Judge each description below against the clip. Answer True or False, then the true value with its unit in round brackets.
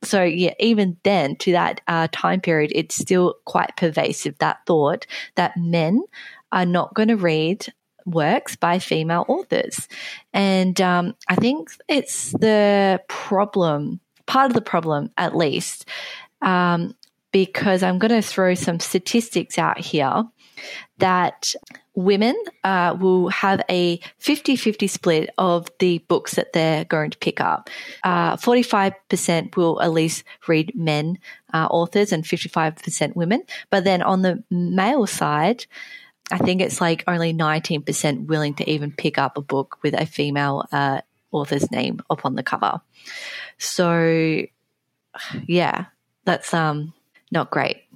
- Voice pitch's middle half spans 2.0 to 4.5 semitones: True (3.9 semitones)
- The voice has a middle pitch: True (180 Hz)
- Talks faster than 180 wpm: False (140 wpm)